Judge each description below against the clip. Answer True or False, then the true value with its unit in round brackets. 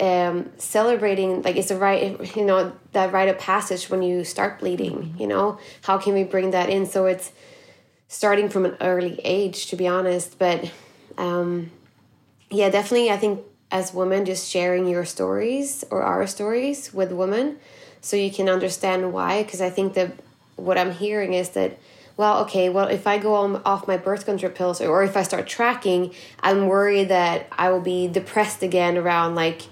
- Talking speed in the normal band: True (190 wpm)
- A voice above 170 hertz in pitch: True (190 Hz)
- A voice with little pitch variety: True (1.9 semitones)